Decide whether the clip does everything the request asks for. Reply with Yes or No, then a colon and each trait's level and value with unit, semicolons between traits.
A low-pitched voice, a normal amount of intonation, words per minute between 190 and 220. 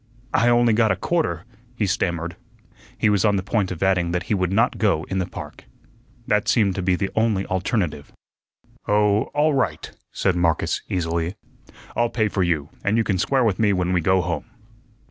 Yes: very low, 95 Hz; average, 3.6 semitones; average, 195 wpm